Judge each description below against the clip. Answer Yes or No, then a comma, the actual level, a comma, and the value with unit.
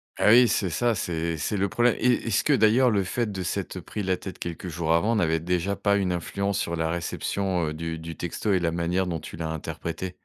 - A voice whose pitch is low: Yes, very low, 90 Hz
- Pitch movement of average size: Yes, average, 3.4 semitones